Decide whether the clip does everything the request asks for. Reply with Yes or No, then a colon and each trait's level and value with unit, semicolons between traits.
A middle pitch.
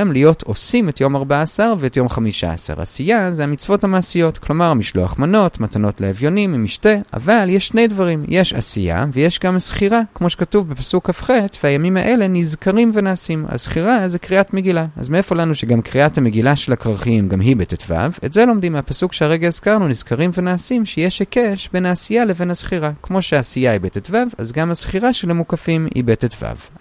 Yes: medium, 170 Hz